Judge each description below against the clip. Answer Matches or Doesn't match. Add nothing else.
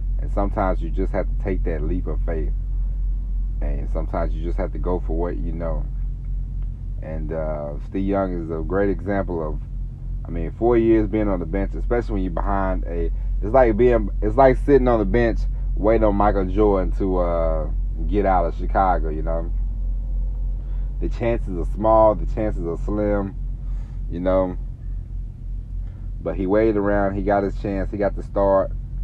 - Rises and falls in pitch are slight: Doesn't match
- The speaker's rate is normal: Matches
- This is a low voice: Matches